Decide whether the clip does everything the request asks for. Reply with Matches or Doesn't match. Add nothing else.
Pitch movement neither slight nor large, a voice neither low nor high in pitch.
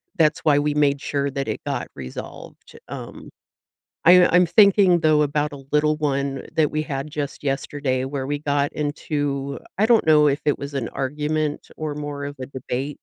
Doesn't match